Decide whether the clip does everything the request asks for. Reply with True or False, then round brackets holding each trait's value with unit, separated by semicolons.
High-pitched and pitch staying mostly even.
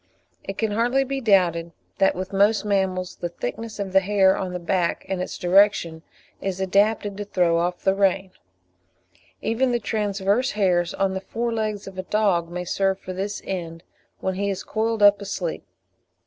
True (195 Hz; 2.2 semitones)